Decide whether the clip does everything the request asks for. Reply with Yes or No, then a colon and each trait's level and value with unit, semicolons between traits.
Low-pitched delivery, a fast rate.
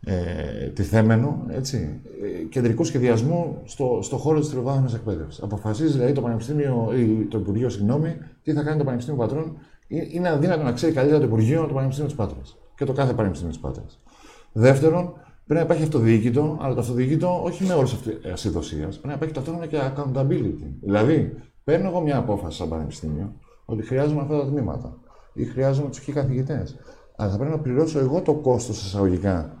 Yes: low, 130 Hz; fast, 175 wpm